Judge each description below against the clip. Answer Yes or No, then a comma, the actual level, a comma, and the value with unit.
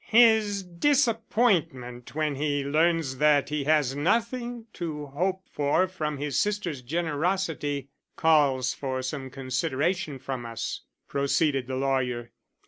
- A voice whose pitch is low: No, medium, 150 Hz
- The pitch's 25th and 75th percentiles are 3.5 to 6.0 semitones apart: Yes, average, 5.2 semitones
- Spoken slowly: Yes, slow, 120 wpm